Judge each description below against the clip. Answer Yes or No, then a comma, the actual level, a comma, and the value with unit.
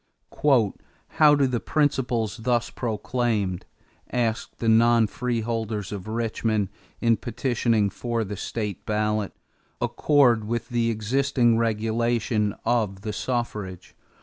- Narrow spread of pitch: Yes, narrow, 2.1 semitones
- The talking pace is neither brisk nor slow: No, slow, 105 wpm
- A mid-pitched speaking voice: No, low, 115 Hz